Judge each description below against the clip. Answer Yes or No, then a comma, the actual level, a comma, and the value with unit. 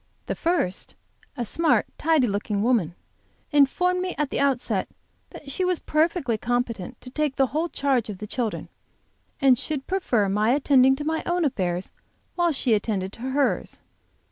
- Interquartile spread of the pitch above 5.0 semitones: Yes, wide, 5.6 semitones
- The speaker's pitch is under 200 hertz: No, very high, 265 Hz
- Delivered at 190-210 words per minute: No, average, 165 wpm